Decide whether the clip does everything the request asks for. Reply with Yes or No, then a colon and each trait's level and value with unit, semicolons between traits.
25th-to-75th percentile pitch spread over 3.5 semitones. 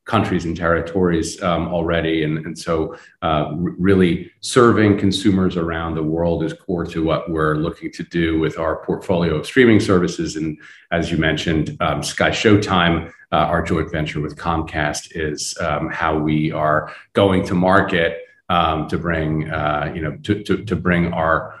No: average, 2.9 semitones